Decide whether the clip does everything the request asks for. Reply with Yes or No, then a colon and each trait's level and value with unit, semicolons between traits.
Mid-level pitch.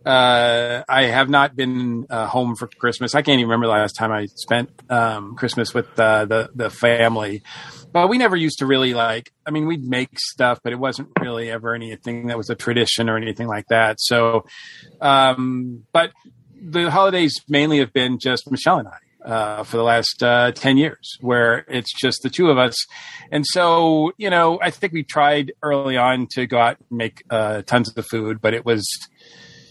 No: low, 125 Hz